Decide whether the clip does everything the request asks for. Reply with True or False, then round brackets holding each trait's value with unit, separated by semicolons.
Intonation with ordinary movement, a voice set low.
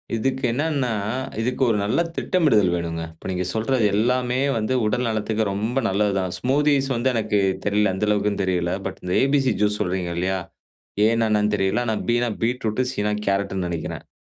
True (4.1 semitones; 110 Hz)